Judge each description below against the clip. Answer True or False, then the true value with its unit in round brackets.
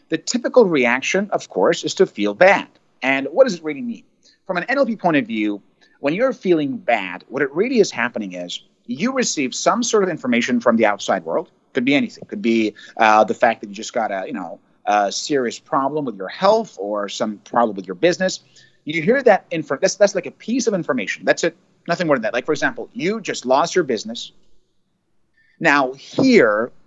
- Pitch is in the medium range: True (170 Hz)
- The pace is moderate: False (210 wpm)